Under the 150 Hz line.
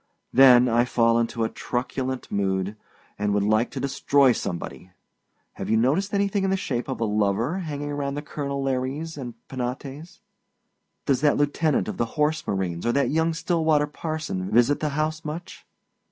Yes: low, 135 Hz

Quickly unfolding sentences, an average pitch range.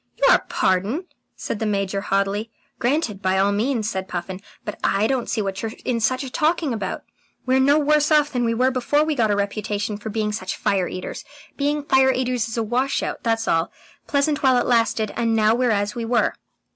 Yes: fast, 210 wpm; average, 4.4 semitones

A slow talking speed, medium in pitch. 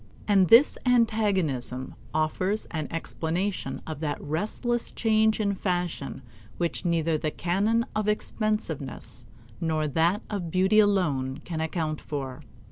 Yes: slow, 125 wpm; medium, 175 Hz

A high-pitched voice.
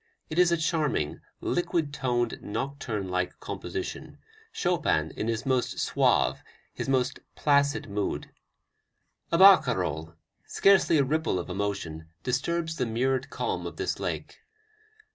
No: low, 130 Hz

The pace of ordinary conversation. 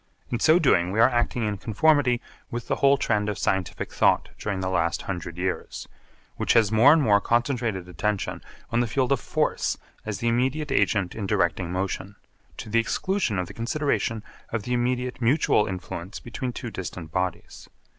Yes: average, 180 wpm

